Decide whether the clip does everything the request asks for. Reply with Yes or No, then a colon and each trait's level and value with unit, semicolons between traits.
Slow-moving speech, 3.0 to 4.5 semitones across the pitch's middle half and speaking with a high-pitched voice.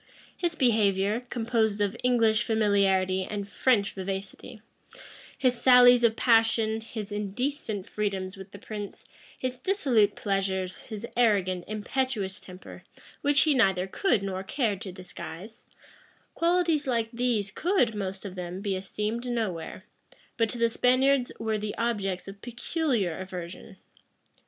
Yes: slow, 130 wpm; average, 4.0 semitones; high, 215 Hz